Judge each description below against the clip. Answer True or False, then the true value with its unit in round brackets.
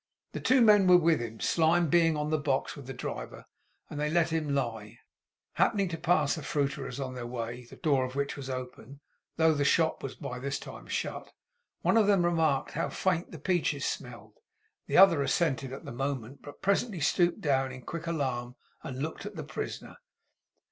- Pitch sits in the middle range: True (145 Hz)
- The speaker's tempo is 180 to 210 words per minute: True (195 wpm)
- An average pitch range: True (4.1 semitones)